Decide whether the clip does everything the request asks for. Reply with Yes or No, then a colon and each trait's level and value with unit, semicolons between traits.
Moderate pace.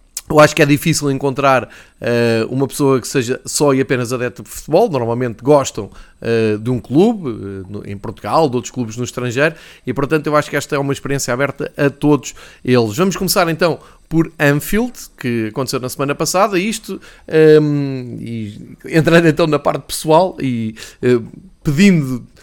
Yes: average, 175 wpm